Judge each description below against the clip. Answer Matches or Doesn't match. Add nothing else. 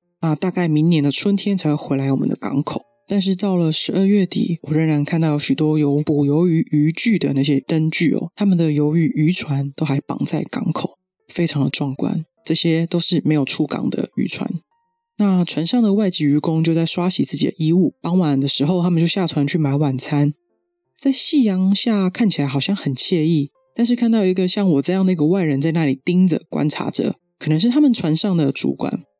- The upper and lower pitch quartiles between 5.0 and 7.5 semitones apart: Doesn't match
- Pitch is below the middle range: Doesn't match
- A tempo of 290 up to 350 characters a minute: Matches